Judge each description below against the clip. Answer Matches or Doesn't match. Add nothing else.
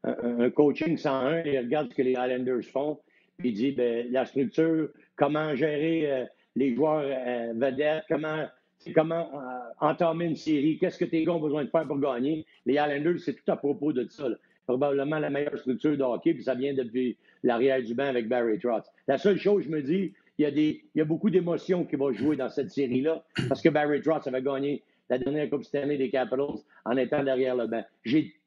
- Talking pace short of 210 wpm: Doesn't match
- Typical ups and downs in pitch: Matches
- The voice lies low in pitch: Doesn't match